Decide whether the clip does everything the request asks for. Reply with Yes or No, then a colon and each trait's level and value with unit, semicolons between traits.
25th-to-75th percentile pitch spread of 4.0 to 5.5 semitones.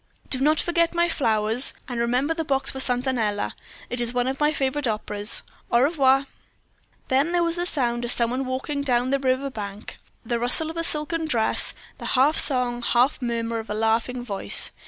No: average, 3.6 semitones